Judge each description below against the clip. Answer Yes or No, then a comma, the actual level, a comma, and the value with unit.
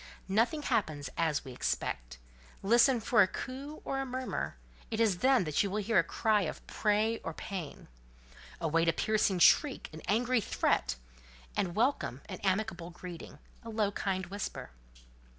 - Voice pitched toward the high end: Yes, high, 205 Hz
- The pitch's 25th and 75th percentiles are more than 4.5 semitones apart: Yes, average, 5.1 semitones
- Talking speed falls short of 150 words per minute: No, average, 155 wpm